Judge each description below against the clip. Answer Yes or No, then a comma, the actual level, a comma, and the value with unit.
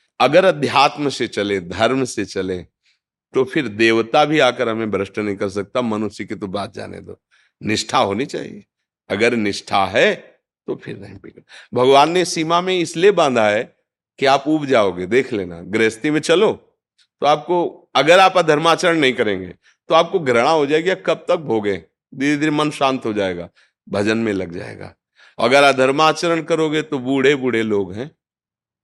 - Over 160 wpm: Yes, average, 170 wpm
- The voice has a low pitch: Yes, low, 130 Hz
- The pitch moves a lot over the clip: Yes, wide, 6.8 semitones